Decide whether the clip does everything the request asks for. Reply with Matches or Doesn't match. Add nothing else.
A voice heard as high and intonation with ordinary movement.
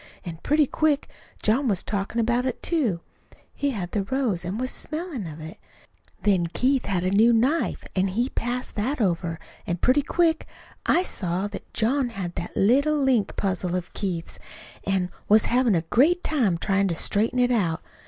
Doesn't match